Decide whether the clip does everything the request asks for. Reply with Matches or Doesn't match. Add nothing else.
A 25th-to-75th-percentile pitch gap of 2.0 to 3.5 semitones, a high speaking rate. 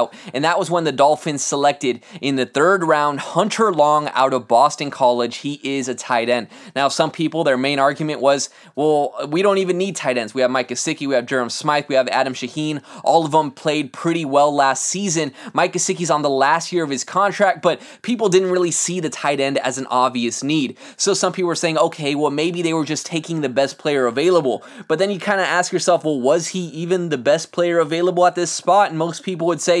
Doesn't match